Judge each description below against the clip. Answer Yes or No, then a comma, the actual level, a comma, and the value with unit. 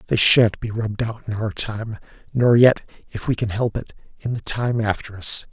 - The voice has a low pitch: Yes, low, 110 Hz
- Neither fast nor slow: No, fast, 215 wpm